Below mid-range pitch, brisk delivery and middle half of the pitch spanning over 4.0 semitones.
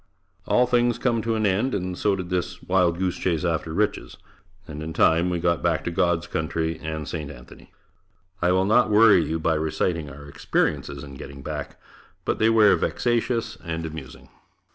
No: very low, 85 Hz; average, 185 wpm; average, 4.6 semitones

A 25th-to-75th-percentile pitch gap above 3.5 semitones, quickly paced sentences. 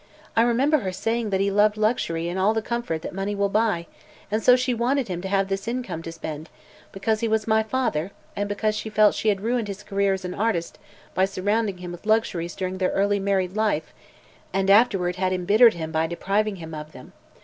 No: average, 3.1 semitones; fast, 220 wpm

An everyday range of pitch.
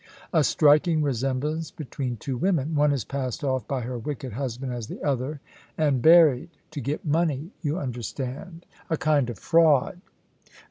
Yes: average, 3.4 semitones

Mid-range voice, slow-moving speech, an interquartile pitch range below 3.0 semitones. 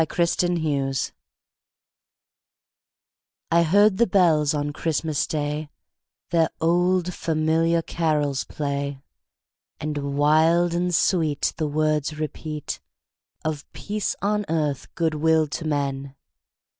Yes: medium, 155 Hz; slow, 105 wpm; narrow, 2.5 semitones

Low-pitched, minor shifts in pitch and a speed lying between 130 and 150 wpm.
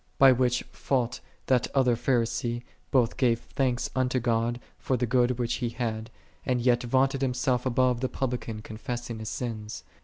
No: low, 125 Hz; narrow, 1.6 semitones; average, 160 wpm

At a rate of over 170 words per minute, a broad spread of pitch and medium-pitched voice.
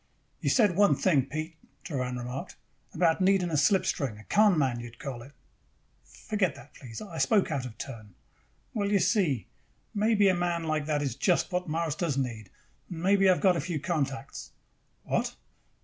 Yes: average, 185 wpm; wide, 5.8 semitones; medium, 160 Hz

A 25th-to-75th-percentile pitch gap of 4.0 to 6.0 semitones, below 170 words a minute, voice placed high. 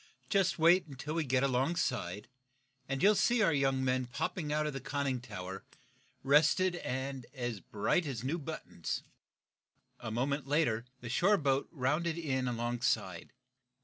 No: average, 4.5 semitones; average, 150 wpm; low, 135 Hz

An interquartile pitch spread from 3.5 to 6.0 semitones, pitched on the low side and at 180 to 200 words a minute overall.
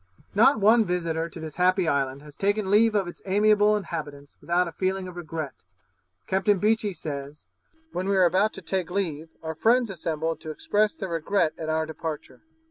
No: average, 4.2 semitones; medium, 180 Hz; average, 185 wpm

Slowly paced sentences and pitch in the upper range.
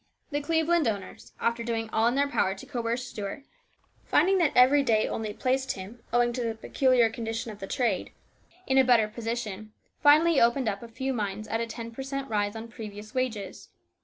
No: average, 195 wpm; high, 235 Hz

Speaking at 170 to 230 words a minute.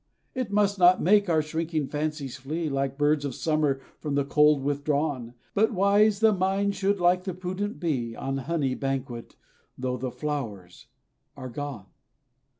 No: average, 155 wpm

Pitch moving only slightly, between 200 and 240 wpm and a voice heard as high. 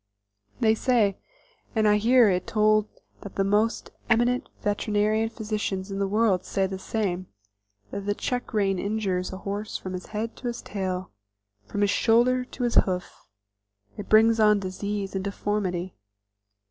No: narrow, 2.3 semitones; average, 160 wpm; high, 210 Hz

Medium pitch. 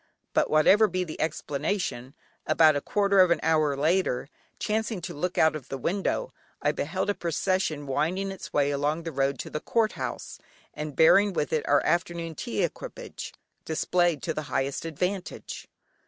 Yes: medium, 160 Hz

